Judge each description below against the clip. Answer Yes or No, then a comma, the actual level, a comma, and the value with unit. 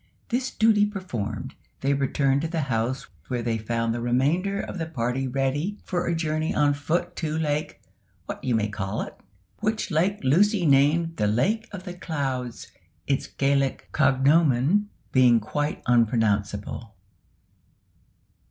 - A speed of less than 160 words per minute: Yes, average, 145 wpm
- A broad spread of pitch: Yes, wide, 5.8 semitones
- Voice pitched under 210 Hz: Yes, medium, 140 Hz